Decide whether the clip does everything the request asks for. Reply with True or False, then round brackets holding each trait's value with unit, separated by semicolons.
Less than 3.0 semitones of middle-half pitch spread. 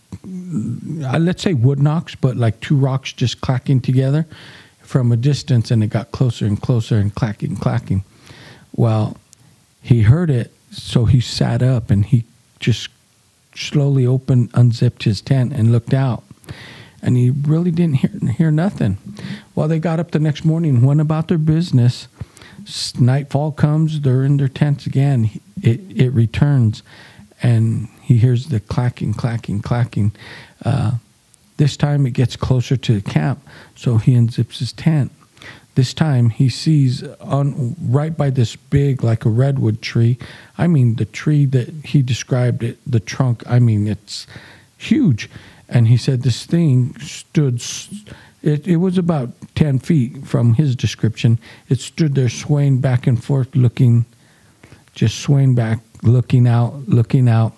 False (3.7 semitones)